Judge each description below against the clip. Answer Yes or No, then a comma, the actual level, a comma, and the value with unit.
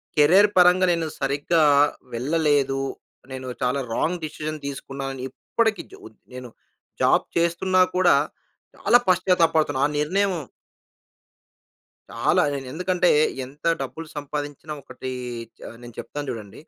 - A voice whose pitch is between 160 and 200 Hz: No, medium, 150 Hz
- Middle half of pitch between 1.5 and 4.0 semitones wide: No, average, 4.6 semitones